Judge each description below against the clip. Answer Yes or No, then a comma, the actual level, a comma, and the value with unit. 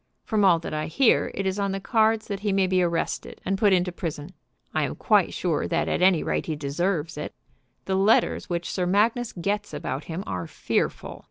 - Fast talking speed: Yes, fast, 210 wpm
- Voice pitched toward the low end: No, medium, 185 Hz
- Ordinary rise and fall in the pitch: Yes, average, 3.3 semitones